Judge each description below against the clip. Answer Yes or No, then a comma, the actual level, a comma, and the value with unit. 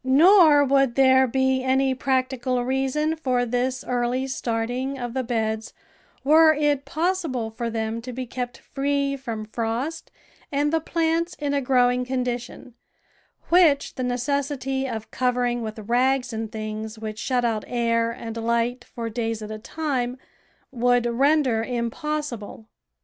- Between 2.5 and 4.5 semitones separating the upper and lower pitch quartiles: Yes, average, 2.9 semitones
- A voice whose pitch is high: Yes, very high, 250 Hz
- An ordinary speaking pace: Yes, average, 145 wpm